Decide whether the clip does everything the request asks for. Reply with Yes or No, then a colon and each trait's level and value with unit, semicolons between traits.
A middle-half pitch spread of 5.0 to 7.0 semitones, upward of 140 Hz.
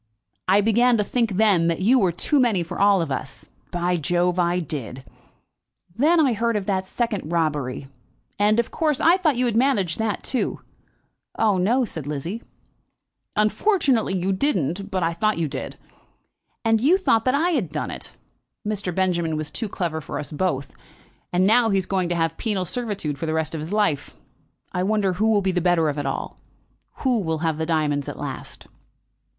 Yes: wide, 5.4 semitones; high, 190 Hz